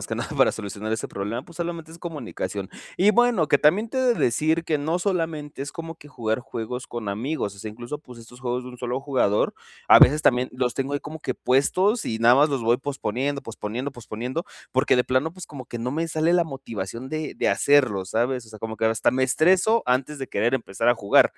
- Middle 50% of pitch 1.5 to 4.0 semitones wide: No, average, 5.3 semitones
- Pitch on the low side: Yes, low, 130 Hz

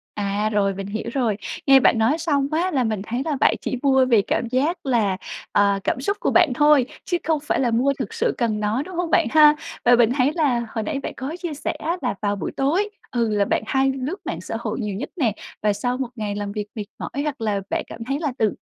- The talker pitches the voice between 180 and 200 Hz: No, very high, 250 Hz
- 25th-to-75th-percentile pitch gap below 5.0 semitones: No, average, 5.3 semitones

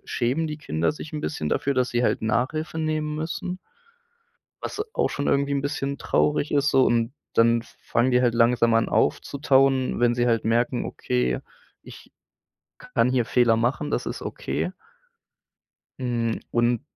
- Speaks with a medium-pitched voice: No, low, 125 Hz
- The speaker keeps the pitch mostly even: No, average, 3.5 semitones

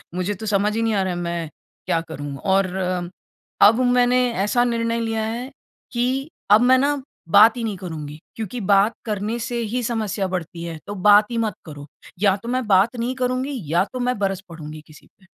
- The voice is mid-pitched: No, high, 215 Hz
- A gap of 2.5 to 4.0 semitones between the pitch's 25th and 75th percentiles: No, average, 4.6 semitones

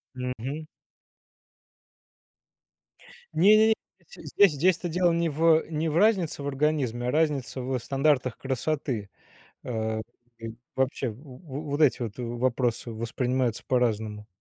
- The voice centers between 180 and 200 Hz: No, low, 135 Hz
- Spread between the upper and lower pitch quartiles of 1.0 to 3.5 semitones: No, average, 4.5 semitones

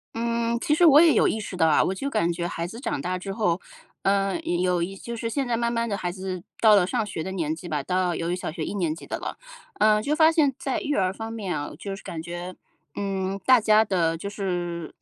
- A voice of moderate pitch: No, high, 195 Hz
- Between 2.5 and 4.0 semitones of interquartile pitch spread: No, average, 4.6 semitones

